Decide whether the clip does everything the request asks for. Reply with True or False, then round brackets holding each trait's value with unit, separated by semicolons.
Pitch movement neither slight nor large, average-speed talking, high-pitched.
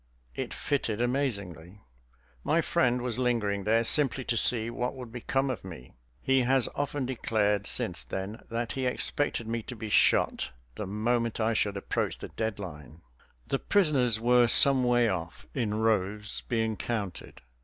False (3.4 semitones; 160 wpm; 115 Hz)